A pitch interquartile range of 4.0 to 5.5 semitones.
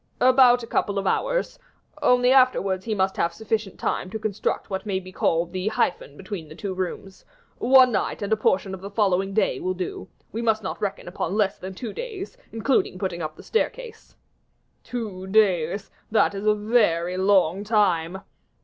No: average, 3.2 semitones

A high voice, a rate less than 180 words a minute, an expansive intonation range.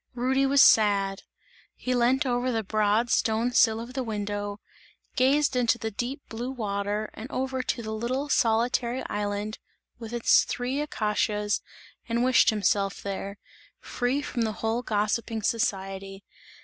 No: high, 225 Hz; average, 145 wpm; average, 3.3 semitones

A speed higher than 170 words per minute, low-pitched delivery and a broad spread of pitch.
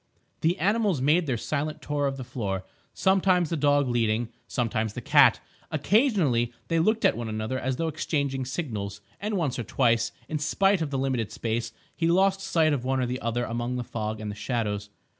Yes: average, 195 wpm; low, 130 Hz; wide, 5.9 semitones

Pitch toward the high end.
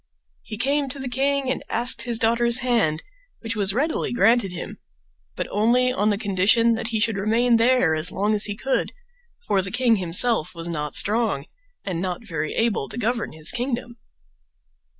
Yes: high, 225 Hz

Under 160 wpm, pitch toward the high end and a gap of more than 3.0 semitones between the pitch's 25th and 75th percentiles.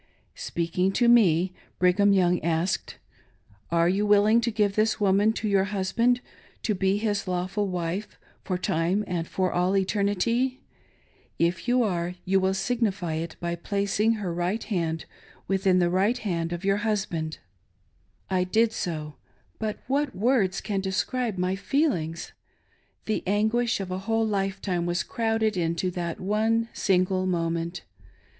Yes: average, 145 wpm; high, 195 Hz; average, 3.4 semitones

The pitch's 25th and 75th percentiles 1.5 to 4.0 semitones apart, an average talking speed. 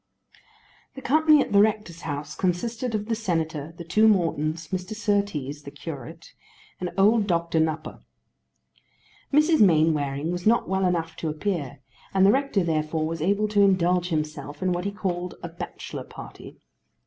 No: average, 4.5 semitones; average, 160 wpm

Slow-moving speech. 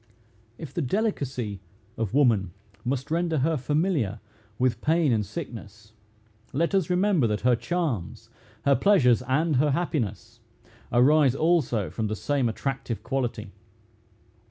Yes: slow, 130 wpm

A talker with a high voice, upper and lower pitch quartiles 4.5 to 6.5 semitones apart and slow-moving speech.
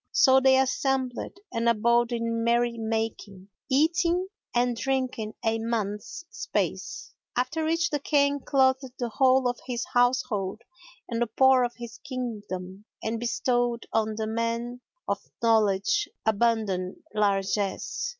No: high, 235 Hz; average, 3.1 semitones; slow, 130 wpm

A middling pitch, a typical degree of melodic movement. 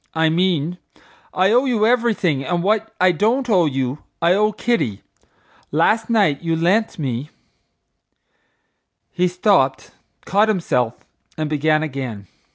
No: medium, 175 Hz; wide, 6.2 semitones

